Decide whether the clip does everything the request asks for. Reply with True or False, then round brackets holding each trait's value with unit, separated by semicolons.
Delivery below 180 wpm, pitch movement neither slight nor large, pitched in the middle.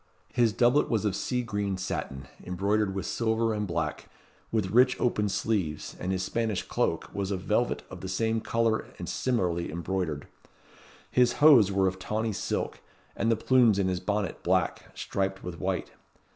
False (170 wpm; 3.4 semitones; 100 Hz)